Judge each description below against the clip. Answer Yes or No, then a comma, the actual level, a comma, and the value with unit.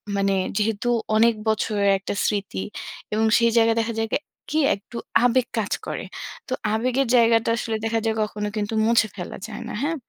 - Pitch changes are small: Yes, narrow, 1.9 semitones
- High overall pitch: Yes, high, 225 Hz